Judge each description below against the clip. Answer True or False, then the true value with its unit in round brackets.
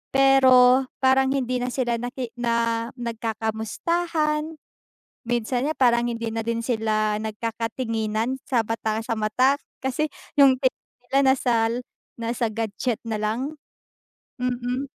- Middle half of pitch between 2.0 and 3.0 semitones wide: True (2.7 semitones)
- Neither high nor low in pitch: False (240 Hz)